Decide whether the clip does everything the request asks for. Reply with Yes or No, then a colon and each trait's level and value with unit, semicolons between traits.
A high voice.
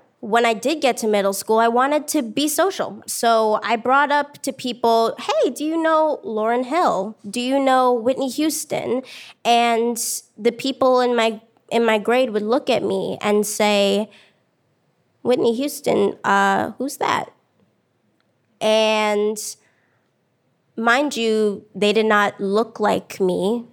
Yes: high, 230 Hz